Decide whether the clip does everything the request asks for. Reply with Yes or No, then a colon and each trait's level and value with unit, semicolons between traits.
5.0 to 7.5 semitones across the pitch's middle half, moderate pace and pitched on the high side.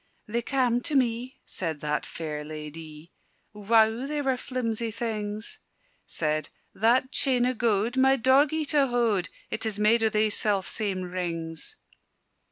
Yes: average, 5.3 semitones; average, 145 wpm; high, 220 Hz